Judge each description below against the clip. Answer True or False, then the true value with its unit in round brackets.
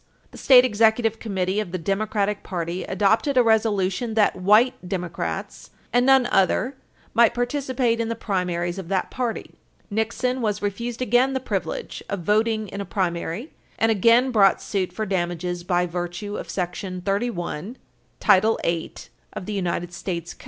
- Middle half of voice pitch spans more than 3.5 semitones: True (4.2 semitones)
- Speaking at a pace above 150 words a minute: False (145 wpm)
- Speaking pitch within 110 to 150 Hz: False (205 Hz)